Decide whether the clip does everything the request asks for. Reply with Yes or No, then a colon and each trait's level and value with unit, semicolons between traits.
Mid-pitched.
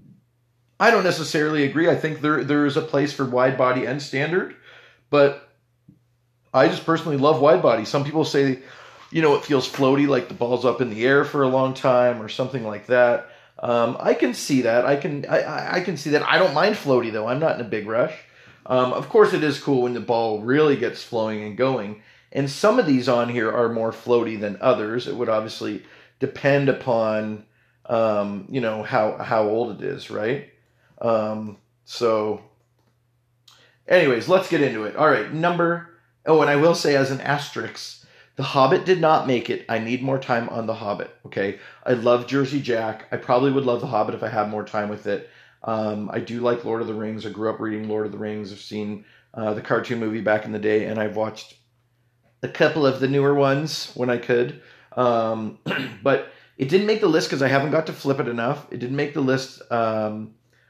No: low, 125 Hz